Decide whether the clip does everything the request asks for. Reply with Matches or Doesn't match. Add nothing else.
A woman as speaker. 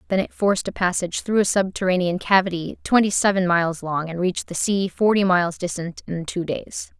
Matches